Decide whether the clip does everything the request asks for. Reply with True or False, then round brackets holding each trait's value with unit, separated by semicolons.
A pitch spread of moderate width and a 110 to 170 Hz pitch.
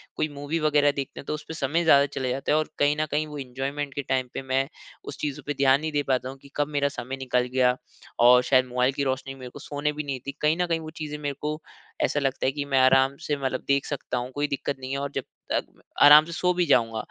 False (2.1 semitones; 140 Hz)